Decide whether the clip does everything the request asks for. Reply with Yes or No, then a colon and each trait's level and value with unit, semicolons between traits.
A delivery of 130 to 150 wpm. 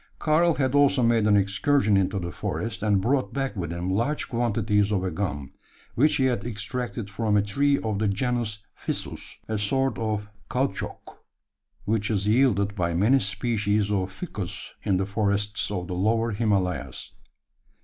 No: average, 165 wpm